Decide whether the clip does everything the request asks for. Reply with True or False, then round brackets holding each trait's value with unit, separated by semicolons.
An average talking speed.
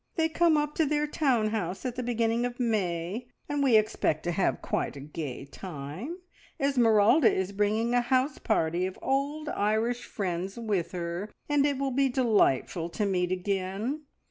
True (170 wpm)